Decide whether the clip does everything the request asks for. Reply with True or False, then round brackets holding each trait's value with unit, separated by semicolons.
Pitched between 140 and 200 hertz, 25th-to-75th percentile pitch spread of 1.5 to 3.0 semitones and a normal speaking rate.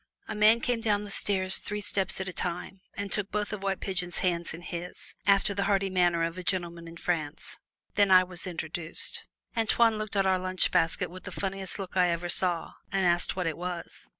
False (185 Hz; 2.4 semitones; 215 wpm)